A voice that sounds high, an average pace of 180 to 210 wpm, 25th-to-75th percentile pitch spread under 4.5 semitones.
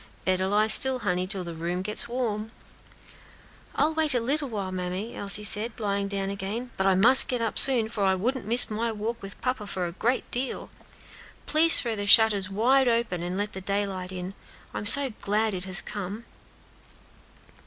Yes: high, 210 Hz; average, 185 wpm; average, 3.6 semitones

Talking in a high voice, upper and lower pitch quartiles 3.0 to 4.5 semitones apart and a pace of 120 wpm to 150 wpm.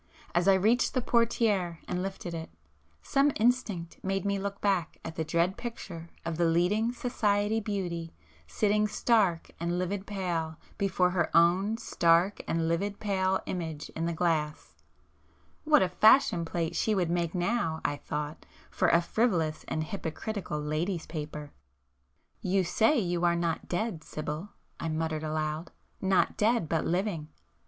No: medium, 180 Hz; average, 3.7 semitones; average, 145 wpm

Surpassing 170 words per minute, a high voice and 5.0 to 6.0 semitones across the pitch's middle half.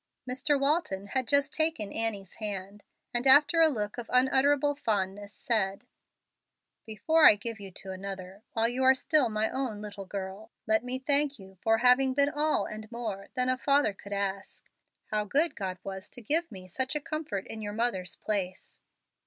Yes: average, 180 wpm; high, 225 Hz; average, 5.3 semitones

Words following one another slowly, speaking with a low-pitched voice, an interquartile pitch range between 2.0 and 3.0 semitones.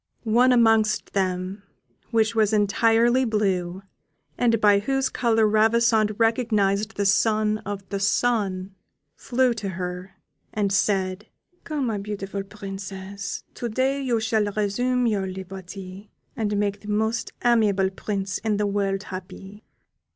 No: slow, 130 wpm; high, 210 Hz; narrow, 2.5 semitones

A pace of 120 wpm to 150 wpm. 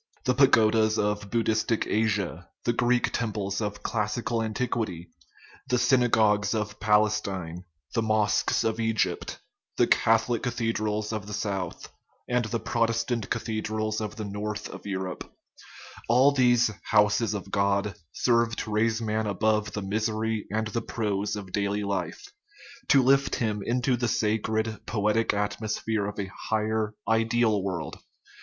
Yes: average, 145 wpm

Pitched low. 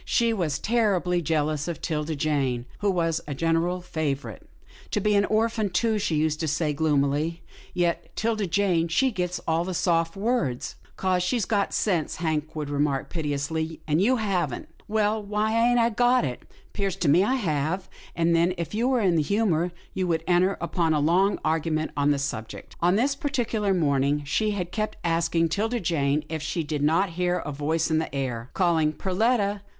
No: medium, 170 Hz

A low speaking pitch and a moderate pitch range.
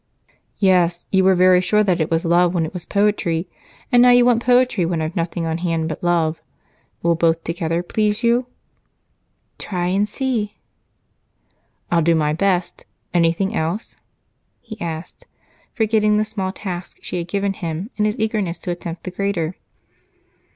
No: medium, 180 Hz; average, 3.9 semitones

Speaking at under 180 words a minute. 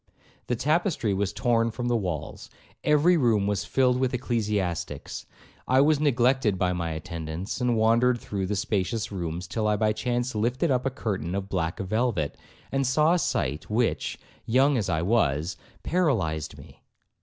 Yes: average, 165 wpm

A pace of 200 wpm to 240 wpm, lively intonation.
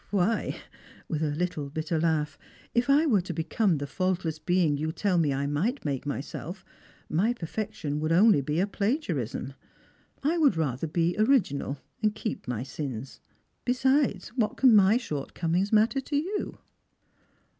No: average, 155 wpm; wide, 6.7 semitones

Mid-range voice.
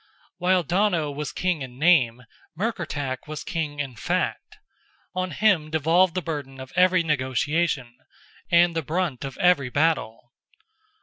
Yes: medium, 155 Hz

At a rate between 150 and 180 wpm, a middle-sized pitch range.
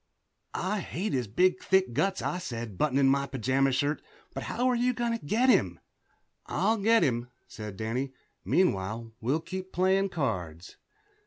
No: average, 160 wpm; wide, 8.3 semitones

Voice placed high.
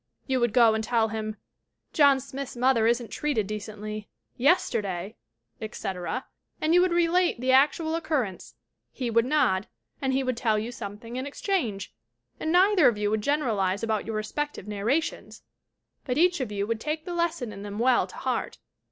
Yes: high, 240 Hz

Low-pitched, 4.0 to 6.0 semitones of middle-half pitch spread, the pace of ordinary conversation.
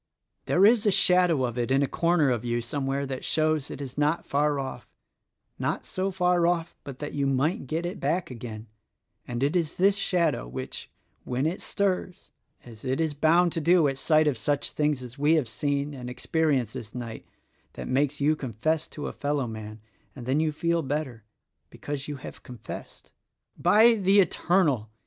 No: medium, 145 Hz; average, 4.6 semitones; average, 195 wpm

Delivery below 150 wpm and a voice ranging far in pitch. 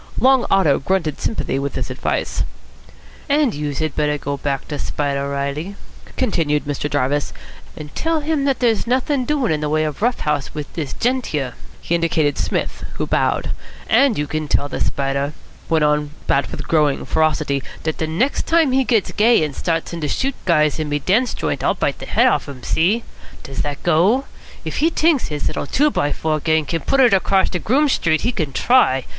No: average, 200 wpm; wide, 8.5 semitones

